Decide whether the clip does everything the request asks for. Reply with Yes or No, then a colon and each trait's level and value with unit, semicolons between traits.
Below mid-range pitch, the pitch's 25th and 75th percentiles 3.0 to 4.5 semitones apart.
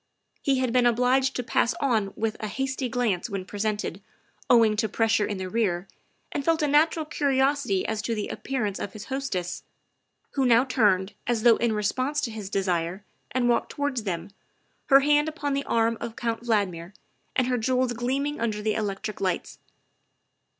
No: high, 230 Hz; average, 4.2 semitones